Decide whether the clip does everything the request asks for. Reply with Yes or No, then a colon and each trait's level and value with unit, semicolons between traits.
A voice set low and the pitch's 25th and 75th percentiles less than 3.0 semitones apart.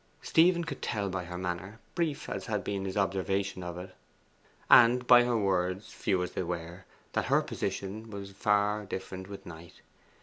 Yes: very low, 95 Hz; narrow, 2.5 semitones